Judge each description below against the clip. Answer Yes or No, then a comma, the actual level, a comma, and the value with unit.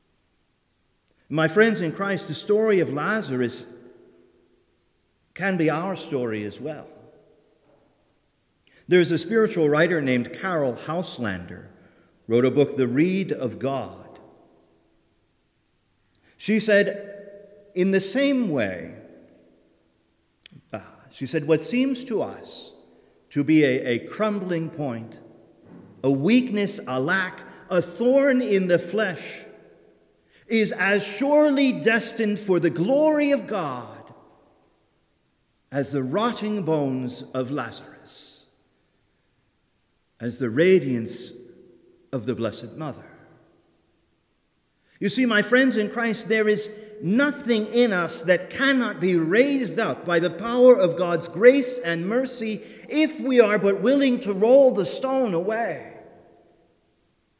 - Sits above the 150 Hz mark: Yes, medium, 185 Hz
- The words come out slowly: Yes, slow, 115 wpm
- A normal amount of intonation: No, wide, 8.3 semitones